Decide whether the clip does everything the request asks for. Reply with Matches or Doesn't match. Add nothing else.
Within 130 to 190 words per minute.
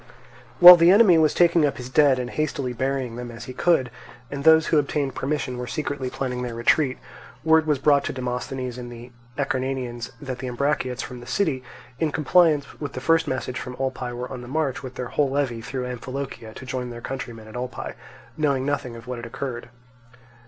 Doesn't match